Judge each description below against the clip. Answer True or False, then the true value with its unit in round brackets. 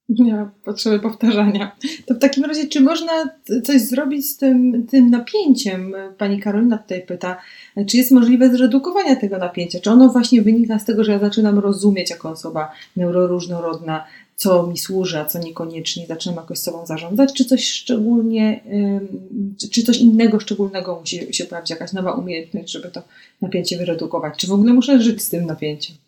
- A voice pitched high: True (205 Hz)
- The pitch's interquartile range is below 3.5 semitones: False (5.5 semitones)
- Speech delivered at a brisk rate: True (170 wpm)